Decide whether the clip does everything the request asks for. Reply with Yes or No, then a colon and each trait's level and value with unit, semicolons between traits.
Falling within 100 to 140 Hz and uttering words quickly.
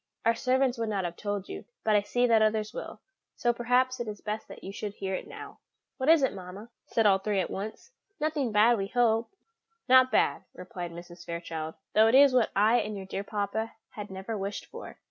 No: high, 215 Hz; fast, 220 wpm